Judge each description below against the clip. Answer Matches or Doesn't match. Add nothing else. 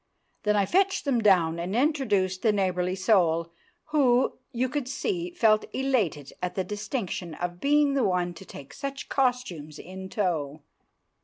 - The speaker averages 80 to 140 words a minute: Doesn't match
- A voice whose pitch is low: Doesn't match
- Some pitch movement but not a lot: Doesn't match